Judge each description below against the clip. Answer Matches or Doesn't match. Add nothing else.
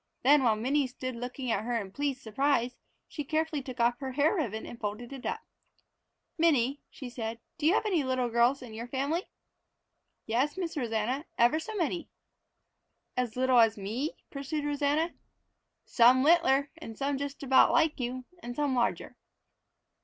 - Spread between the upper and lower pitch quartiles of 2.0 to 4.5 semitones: Matches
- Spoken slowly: Doesn't match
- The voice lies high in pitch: Matches